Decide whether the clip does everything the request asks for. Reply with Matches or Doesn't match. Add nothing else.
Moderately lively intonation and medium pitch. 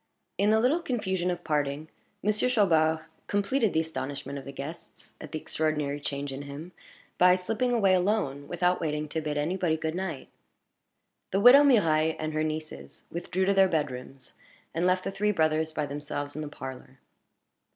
Matches